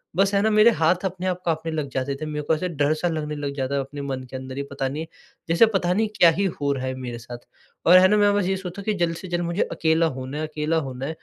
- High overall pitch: No, medium, 160 Hz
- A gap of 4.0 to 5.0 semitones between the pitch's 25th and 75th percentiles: Yes, average, 4.6 semitones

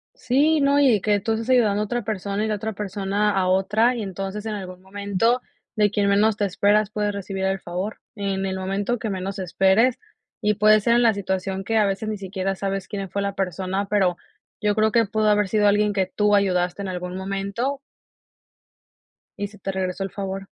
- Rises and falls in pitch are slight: Yes, narrow, 1.8 semitones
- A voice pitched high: Yes, high, 200 Hz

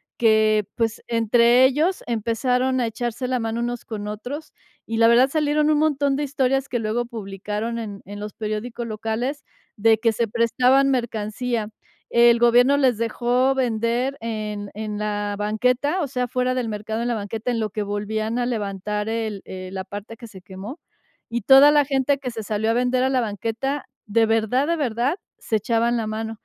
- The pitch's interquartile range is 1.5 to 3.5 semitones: Yes, average, 2.8 semitones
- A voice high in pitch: Yes, high, 230 Hz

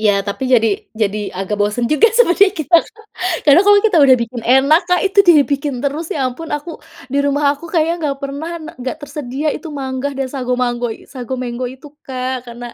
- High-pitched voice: Yes, very high, 275 Hz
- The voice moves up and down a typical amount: Yes, average, 3.8 semitones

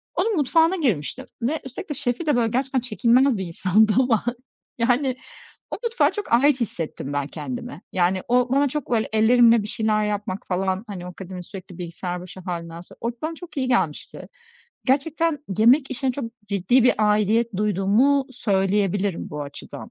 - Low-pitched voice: No, high, 225 Hz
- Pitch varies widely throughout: Yes, wide, 5.8 semitones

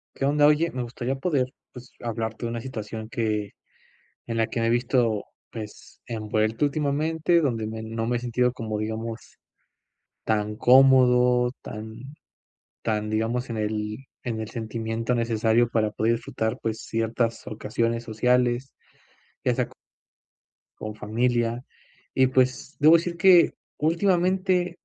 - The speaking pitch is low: Yes, low, 115 Hz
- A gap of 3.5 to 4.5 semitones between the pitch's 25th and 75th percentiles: No, average, 2.8 semitones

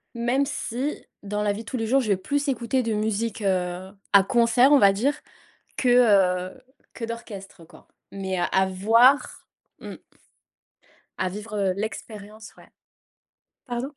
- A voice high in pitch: Yes, high, 220 Hz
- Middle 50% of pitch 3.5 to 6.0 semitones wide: Yes, average, 3.9 semitones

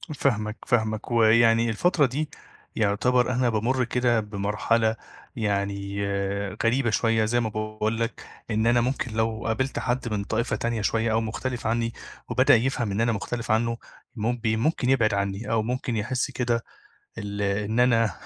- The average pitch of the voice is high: No, low, 115 Hz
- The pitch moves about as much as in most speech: No, narrow, 2.1 semitones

